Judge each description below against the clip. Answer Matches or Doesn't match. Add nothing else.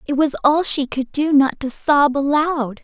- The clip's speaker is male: Doesn't match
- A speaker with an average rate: Doesn't match